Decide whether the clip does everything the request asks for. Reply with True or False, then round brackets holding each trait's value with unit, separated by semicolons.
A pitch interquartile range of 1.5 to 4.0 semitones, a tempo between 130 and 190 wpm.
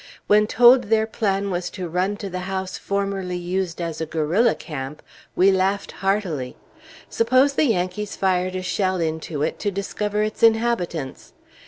True (2.9 semitones; 160 wpm)